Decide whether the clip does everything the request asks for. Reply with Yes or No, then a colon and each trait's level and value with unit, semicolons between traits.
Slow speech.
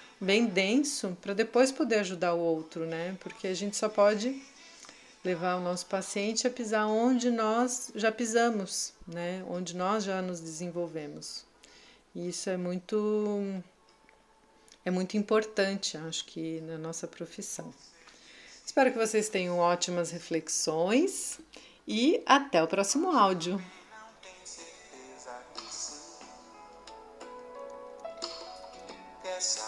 Yes: slow, 105 wpm